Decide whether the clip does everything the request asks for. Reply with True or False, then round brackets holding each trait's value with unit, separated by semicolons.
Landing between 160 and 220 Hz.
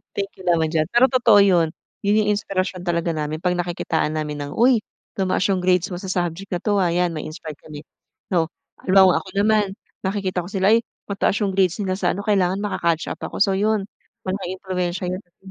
True (185 Hz)